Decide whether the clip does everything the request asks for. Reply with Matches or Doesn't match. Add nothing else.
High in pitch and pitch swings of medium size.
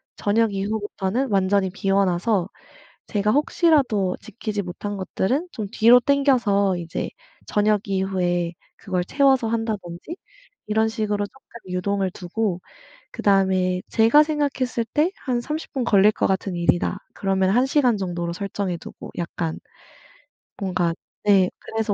Matches